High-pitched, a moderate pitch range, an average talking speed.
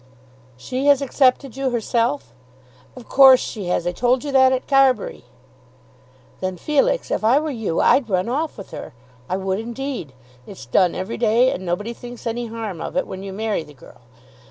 No: high, 235 Hz; wide, 5.7 semitones; average, 185 wpm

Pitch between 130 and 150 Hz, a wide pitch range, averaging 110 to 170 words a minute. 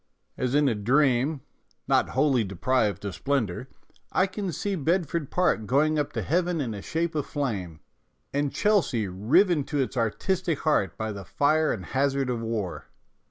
No: medium, 140 Hz; wide, 5.9 semitones; average, 180 wpm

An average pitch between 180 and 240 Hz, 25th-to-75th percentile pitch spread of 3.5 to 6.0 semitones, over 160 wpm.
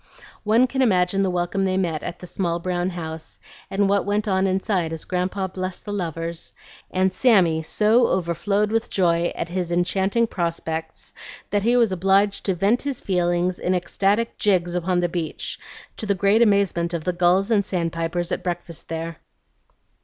No: medium, 185 Hz; narrow, 2.6 semitones; average, 175 wpm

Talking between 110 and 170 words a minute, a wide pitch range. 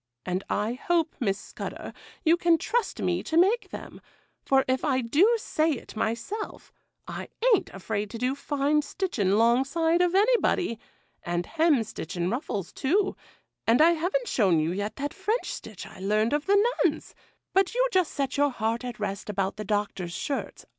Yes: average, 165 wpm; wide, 8.4 semitones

